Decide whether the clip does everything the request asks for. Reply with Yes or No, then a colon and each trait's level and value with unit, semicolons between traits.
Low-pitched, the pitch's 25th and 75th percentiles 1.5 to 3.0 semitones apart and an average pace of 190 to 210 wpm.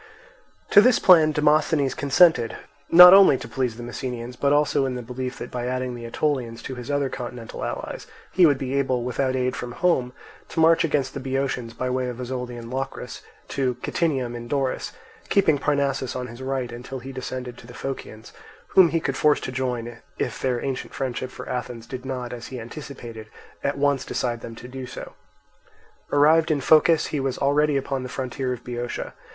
Yes: low, 130 Hz; narrow, 2.6 semitones; average, 195 wpm